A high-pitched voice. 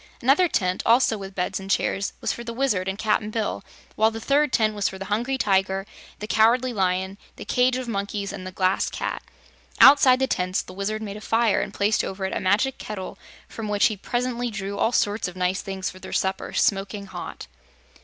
Yes: high, 205 Hz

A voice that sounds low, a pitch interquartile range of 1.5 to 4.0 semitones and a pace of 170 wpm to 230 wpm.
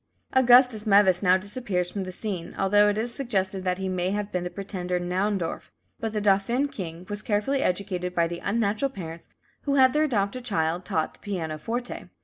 No: high, 200 Hz; average, 3.6 semitones; average, 185 wpm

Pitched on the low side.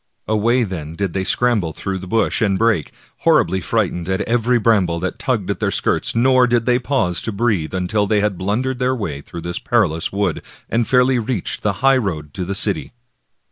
Yes: low, 105 Hz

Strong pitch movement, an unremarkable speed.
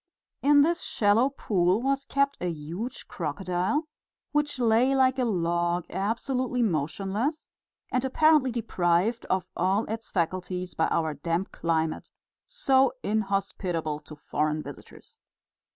No: wide, 7.1 semitones; slow, 120 wpm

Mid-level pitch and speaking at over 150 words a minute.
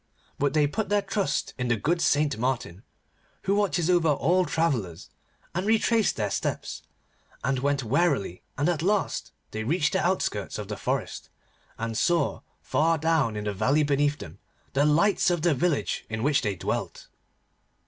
Yes: medium, 145 Hz; average, 170 wpm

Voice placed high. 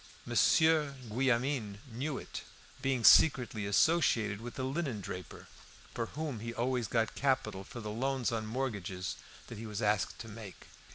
No: low, 115 Hz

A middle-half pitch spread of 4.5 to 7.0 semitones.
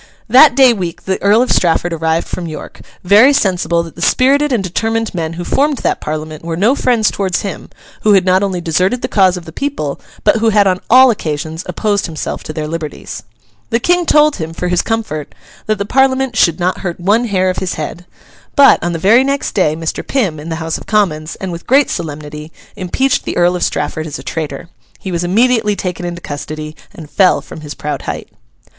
Yes: wide, 5.5 semitones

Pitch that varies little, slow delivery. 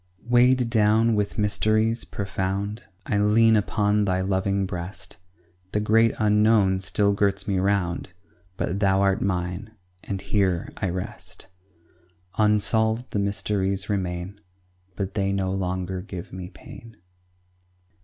Yes: narrow, 2.1 semitones; slow, 125 wpm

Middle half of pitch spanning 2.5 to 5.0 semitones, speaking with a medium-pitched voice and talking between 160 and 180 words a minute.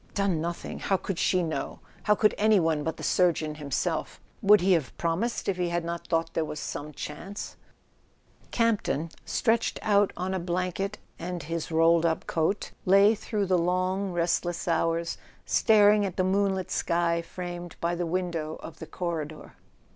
Yes: average, 2.8 semitones; medium, 175 Hz; average, 170 wpm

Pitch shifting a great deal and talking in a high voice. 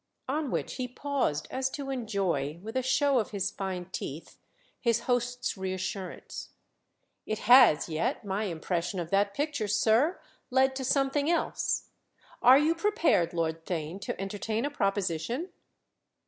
Yes: wide, 6.1 semitones; high, 220 Hz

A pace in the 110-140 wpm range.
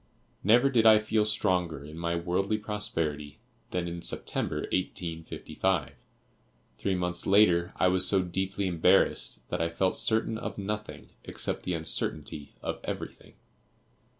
Yes: slow, 135 wpm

